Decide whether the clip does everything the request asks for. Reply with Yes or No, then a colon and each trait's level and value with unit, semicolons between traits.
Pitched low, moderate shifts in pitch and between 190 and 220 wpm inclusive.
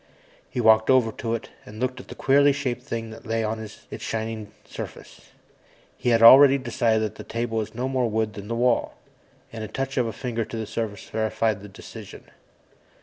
No: low, 115 Hz; narrow, 2.2 semitones; fast, 205 wpm